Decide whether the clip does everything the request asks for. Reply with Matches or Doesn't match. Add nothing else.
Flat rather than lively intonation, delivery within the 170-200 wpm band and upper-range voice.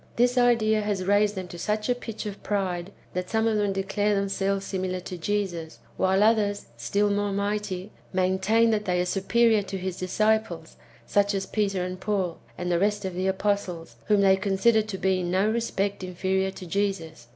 Matches